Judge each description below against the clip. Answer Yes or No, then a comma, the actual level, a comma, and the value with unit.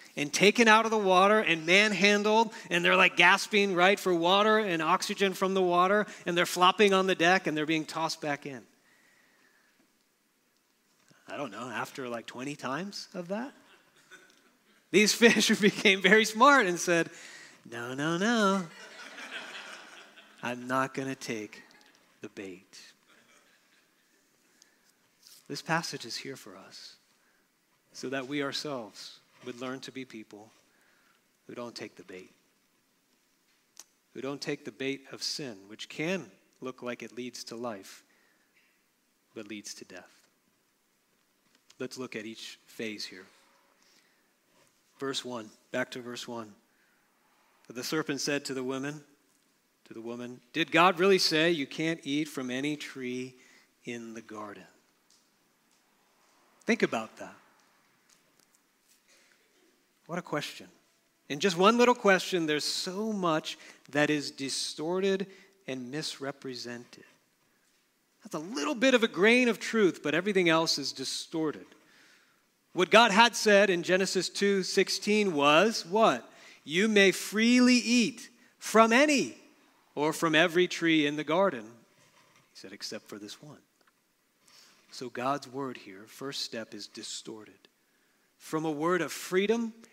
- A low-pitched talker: No, medium, 160 Hz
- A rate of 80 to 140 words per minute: Yes, slow, 135 wpm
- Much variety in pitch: Yes, wide, 6.8 semitones